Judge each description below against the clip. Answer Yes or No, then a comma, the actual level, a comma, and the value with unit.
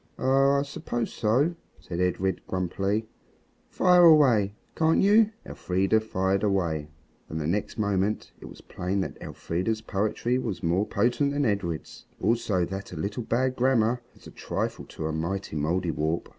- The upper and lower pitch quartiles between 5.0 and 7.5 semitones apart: Yes, average, 5.3 semitones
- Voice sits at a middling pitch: No, low, 100 Hz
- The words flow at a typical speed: Yes, average, 155 wpm